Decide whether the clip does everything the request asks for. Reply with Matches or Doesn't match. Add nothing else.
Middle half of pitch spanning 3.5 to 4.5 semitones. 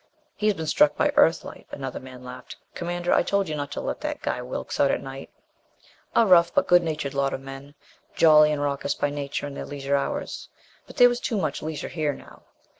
Matches